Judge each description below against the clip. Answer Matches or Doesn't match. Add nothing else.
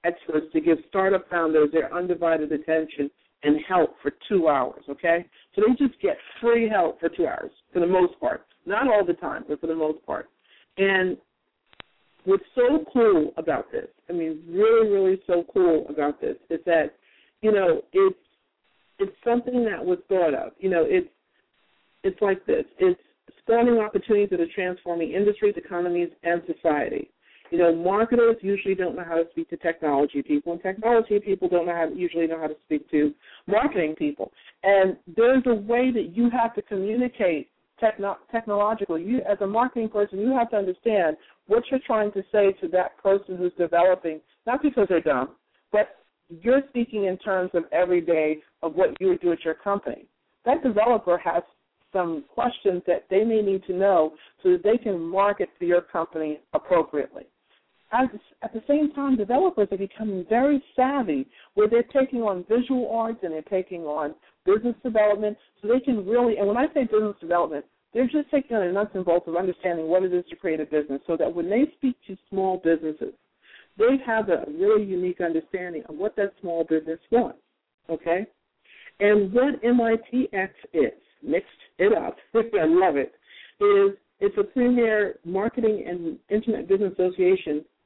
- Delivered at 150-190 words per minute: Matches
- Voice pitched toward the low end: Doesn't match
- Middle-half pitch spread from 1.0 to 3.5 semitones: Doesn't match